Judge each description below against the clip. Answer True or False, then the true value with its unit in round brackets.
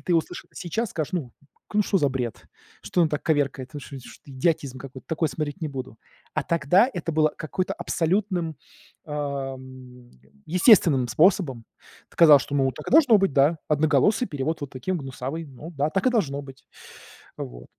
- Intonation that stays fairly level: False (4.3 semitones)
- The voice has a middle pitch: True (150 Hz)